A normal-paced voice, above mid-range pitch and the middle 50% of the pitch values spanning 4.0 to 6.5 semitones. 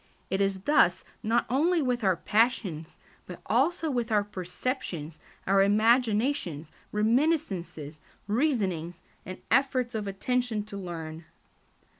No: slow, 115 wpm; high, 210 Hz; wide, 5.5 semitones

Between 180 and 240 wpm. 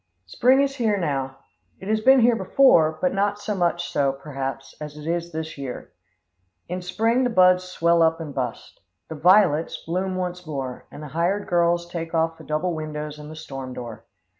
Yes: average, 190 wpm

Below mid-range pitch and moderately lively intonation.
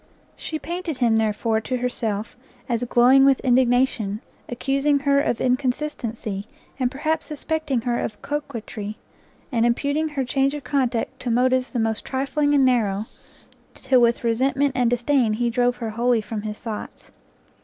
No: very high, 250 Hz; average, 3.3 semitones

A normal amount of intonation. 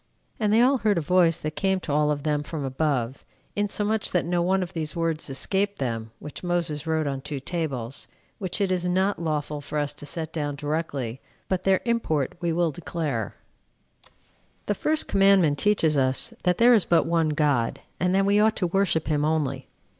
Yes: average, 4.5 semitones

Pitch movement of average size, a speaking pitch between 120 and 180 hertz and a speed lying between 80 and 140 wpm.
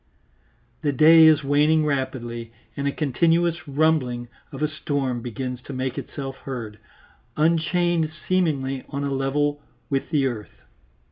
Yes: average, 3.2 semitones; medium, 140 Hz; slow, 135 wpm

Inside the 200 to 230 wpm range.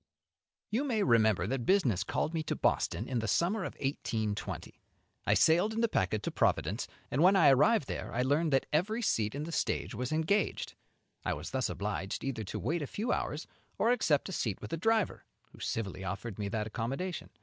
Yes: fast, 205 wpm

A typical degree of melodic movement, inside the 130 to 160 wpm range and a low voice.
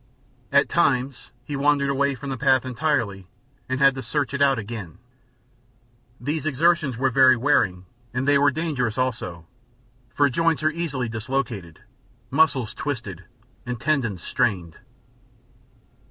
Yes: average, 4.0 semitones; slow, 135 wpm; low, 130 Hz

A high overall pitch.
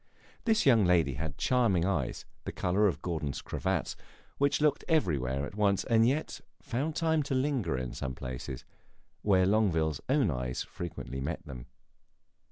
No: very low, 95 Hz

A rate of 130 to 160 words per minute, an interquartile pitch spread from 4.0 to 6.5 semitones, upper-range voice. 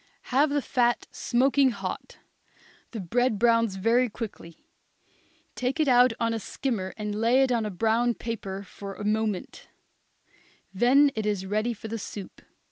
No: average, 155 wpm; average, 3.1 semitones; high, 230 Hz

